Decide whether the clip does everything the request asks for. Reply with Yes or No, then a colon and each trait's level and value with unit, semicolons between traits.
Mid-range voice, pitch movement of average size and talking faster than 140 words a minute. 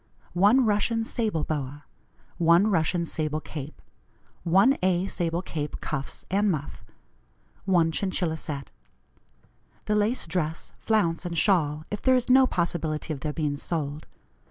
No: medium, 170 Hz; average, 4.7 semitones; slow, 135 wpm